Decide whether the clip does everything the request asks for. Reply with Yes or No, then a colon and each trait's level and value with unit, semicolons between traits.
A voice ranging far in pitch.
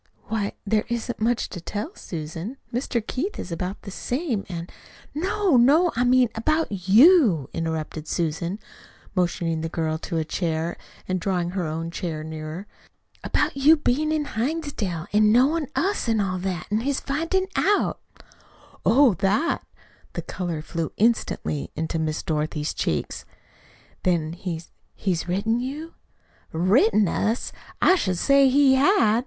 Yes: wide, 8.0 semitones